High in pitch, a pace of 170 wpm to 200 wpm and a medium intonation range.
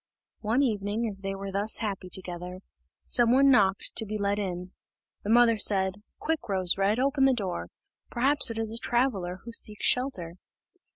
Yes: high, 210 Hz; average, 175 wpm; average, 3.9 semitones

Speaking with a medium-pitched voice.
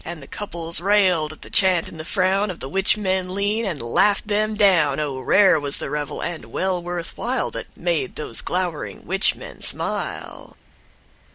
Yes: medium, 180 Hz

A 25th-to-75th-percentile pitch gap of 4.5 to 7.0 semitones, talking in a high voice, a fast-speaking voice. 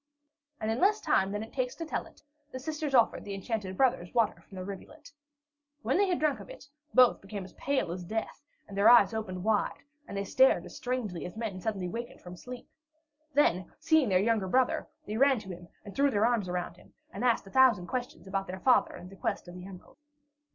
Yes: average, 5.3 semitones; high, 220 Hz; fast, 225 wpm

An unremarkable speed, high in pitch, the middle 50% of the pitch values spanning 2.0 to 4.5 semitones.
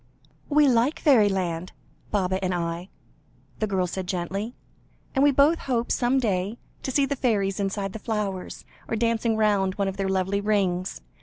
Yes: average, 165 wpm; high, 200 Hz; average, 3.8 semitones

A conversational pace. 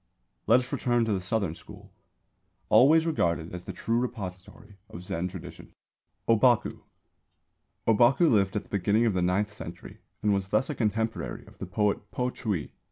Yes: average, 170 wpm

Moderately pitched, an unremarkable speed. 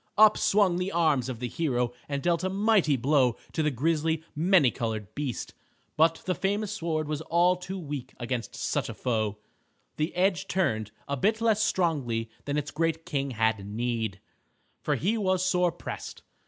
Yes: medium, 155 Hz; average, 175 wpm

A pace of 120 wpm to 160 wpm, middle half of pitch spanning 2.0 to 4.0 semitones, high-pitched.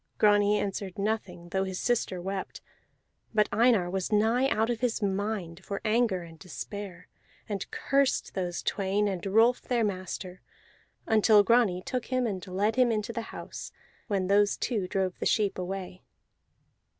Yes: average, 155 wpm; average, 3.0 semitones; high, 205 Hz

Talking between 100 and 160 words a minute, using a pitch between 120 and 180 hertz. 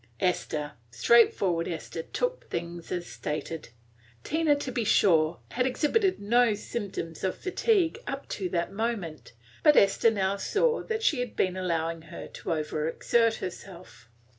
No: average, 145 wpm; high, 195 Hz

